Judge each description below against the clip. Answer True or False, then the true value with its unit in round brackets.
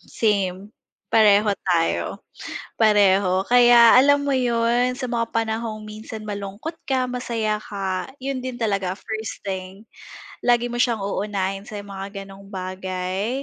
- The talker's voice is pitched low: False (215 Hz)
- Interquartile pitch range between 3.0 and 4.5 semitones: True (3.6 semitones)